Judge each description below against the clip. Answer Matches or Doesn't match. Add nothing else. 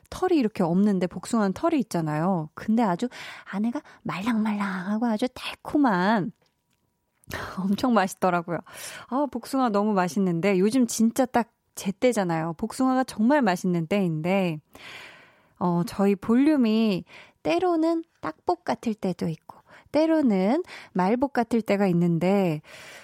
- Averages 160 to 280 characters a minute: Matches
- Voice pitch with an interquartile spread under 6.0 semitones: Matches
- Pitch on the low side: Doesn't match